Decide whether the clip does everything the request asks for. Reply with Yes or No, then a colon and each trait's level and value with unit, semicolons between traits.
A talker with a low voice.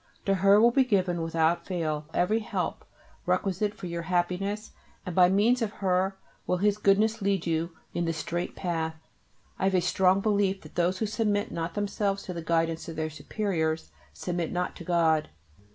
No: medium, 180 Hz